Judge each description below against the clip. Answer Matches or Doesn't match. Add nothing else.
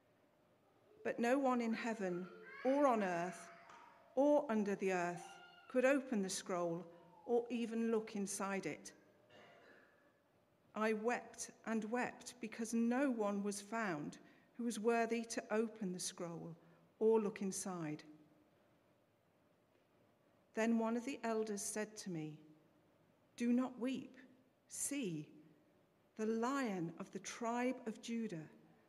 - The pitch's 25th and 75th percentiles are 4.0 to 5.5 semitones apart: Matches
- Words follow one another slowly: Matches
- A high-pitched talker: Matches